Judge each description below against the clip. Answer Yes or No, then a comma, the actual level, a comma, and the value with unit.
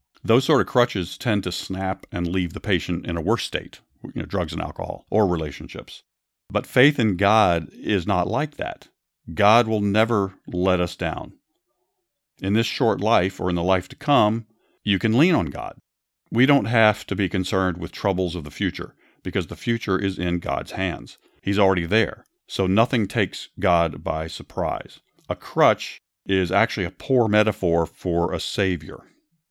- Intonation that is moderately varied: Yes, average, 3.8 semitones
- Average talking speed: Yes, average, 180 wpm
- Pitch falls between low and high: No, very low, 95 Hz